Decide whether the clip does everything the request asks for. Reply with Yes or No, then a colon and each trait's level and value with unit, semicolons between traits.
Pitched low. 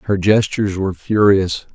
Yes: low, 100 Hz